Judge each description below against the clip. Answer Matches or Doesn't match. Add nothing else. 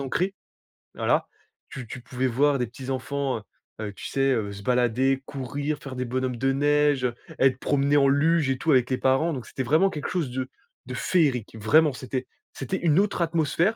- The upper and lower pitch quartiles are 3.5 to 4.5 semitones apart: Doesn't match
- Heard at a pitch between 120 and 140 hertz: Matches